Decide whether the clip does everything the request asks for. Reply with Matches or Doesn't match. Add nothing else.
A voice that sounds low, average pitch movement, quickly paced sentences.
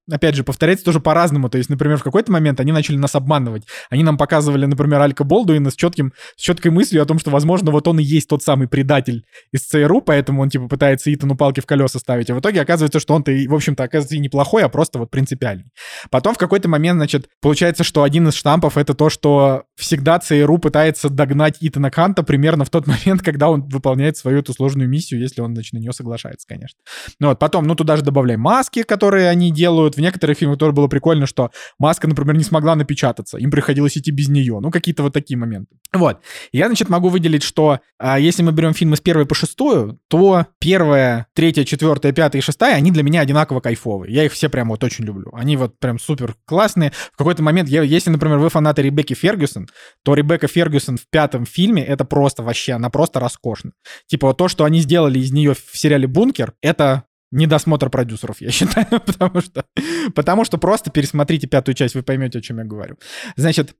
Doesn't match